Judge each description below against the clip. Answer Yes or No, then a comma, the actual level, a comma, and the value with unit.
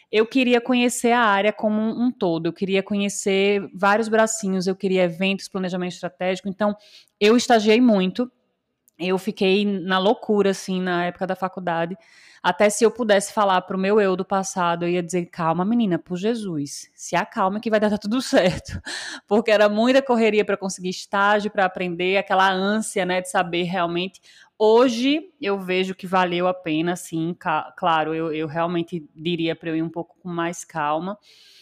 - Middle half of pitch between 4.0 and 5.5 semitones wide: No, average, 3.1 semitones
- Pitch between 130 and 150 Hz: No, high, 195 Hz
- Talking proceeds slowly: No, average, 175 wpm